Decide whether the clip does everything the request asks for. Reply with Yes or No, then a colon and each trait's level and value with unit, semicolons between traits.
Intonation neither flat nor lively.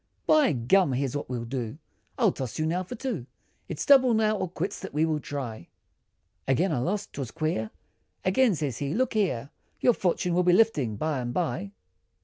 No: wide, 7.4 semitones